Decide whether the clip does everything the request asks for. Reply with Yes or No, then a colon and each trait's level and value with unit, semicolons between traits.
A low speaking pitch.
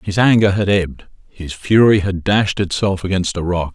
Yes: very low, 95 Hz